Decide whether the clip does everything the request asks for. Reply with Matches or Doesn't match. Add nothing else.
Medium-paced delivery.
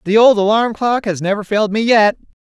Doesn't match